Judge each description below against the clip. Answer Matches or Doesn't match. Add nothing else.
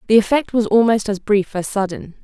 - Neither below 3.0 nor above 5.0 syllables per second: Doesn't match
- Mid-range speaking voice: Doesn't match